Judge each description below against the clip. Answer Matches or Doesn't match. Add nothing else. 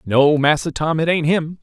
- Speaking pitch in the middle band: Matches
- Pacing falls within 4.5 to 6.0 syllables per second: Matches